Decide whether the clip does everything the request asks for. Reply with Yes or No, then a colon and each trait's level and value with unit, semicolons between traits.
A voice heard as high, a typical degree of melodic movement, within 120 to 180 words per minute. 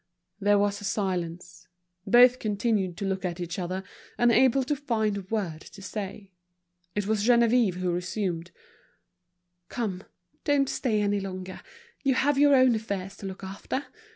Yes: high, 205 Hz; average, 4.1 semitones; average, 155 wpm